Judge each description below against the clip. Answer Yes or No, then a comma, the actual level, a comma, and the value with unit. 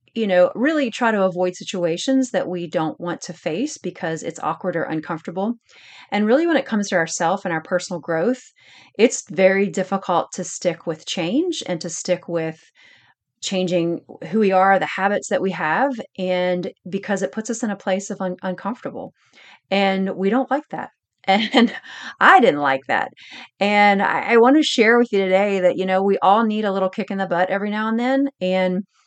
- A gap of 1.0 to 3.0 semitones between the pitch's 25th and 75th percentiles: No, average, 3.9 semitones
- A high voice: Yes, high, 195 Hz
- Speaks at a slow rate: No, average, 200 wpm